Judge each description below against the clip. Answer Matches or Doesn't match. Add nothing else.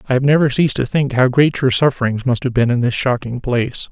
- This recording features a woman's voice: Doesn't match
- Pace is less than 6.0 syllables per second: Doesn't match